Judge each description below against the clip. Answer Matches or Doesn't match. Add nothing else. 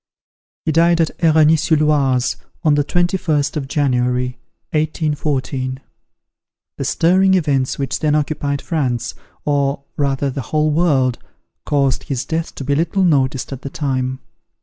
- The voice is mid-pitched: Matches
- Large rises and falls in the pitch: Doesn't match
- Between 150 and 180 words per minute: Doesn't match